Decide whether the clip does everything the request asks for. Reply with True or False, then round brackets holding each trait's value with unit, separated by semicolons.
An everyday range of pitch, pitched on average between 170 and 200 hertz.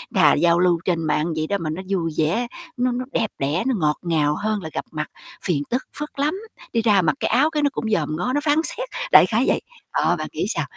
False (7.9 semitones; 190 Hz)